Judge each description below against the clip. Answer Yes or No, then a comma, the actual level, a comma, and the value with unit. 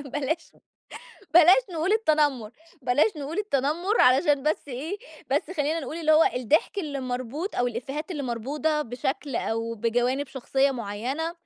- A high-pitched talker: Yes, very high, 285 Hz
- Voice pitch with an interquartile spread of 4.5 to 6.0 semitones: No, average, 4.1 semitones